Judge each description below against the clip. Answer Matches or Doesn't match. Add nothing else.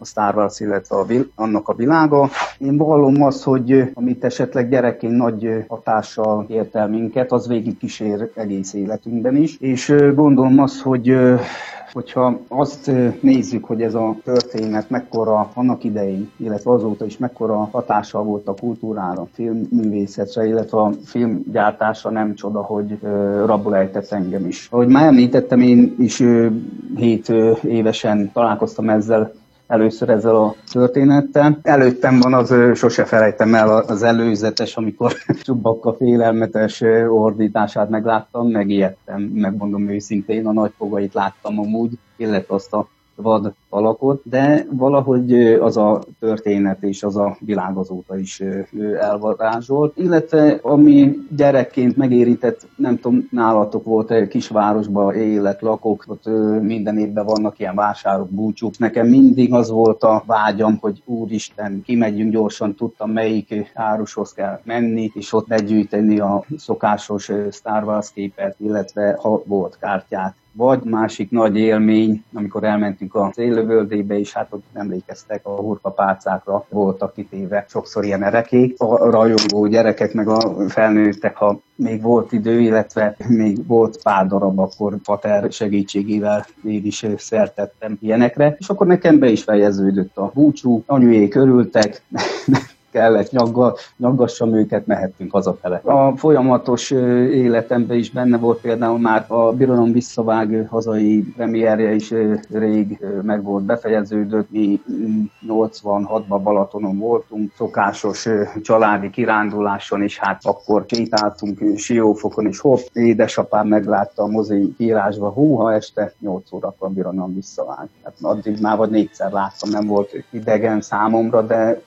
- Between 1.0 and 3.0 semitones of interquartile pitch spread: Matches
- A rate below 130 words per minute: Doesn't match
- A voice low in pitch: Matches